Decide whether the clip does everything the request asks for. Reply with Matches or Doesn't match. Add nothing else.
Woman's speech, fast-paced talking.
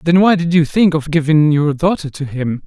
Doesn't match